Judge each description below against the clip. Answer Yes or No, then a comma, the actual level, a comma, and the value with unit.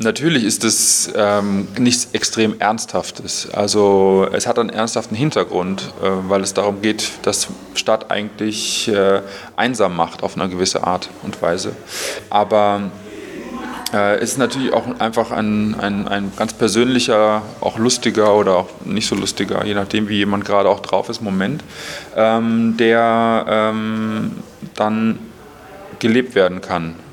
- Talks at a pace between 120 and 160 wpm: Yes, average, 145 wpm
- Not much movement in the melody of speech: Yes, narrow, 2.1 semitones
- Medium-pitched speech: No, low, 110 Hz